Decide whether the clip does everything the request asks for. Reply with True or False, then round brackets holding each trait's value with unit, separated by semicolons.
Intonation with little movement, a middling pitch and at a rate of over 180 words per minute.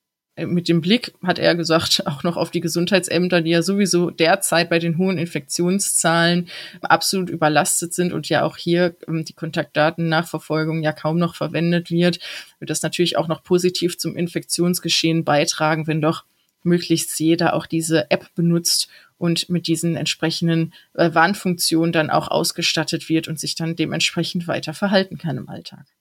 False (1.5 semitones; 170 Hz; 155 wpm)